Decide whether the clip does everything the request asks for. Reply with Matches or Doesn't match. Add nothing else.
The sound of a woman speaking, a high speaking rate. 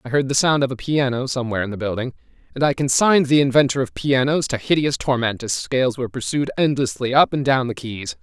Doesn't match